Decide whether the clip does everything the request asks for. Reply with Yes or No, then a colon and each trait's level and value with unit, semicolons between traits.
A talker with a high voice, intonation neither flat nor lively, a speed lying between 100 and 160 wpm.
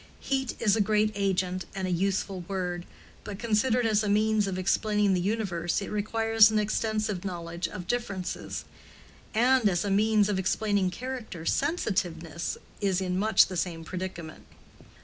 Yes: high, 200 Hz; average, 3.1 semitones; average, 155 wpm